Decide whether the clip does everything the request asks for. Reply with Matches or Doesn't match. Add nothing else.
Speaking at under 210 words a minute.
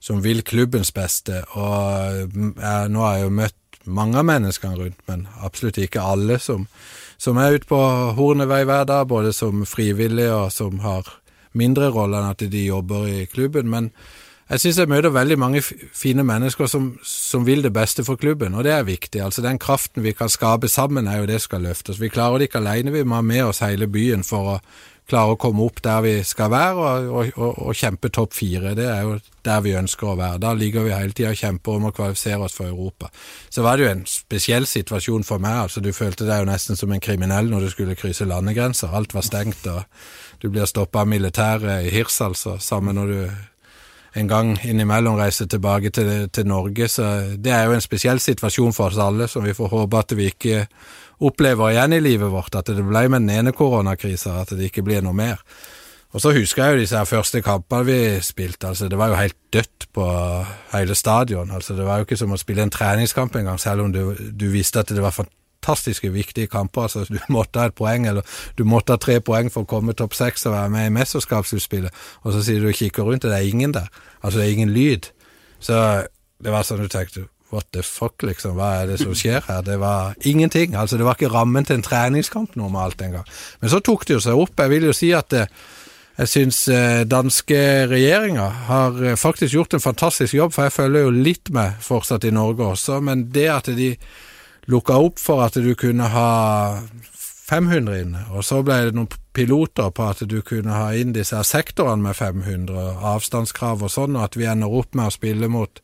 Doesn't match